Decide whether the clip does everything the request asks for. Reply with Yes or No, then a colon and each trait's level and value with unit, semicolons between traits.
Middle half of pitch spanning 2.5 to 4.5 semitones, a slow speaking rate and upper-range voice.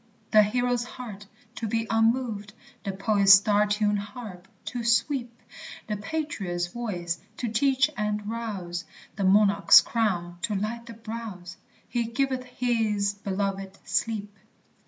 Yes: average, 2.9 semitones; slow, 130 wpm; high, 210 Hz